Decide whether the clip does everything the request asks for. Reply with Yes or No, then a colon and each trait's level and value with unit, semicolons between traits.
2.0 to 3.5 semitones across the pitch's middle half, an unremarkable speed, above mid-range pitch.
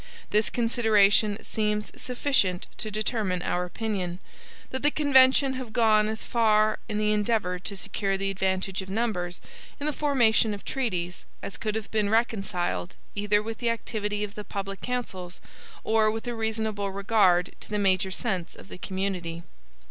Yes: average, 2.7 semitones; average, 165 wpm; high, 210 Hz